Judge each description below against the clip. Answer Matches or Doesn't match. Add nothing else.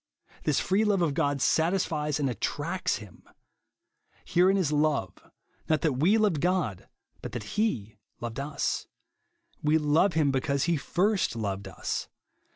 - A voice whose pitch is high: Doesn't match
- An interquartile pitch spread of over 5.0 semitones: Matches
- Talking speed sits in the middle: Matches